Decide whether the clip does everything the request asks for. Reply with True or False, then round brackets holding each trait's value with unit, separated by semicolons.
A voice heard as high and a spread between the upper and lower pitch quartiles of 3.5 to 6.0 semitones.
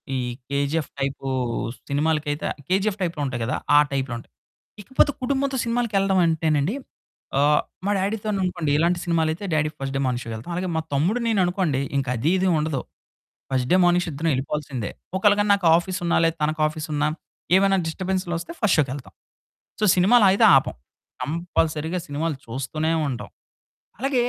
False (165 Hz; 4.9 semitones)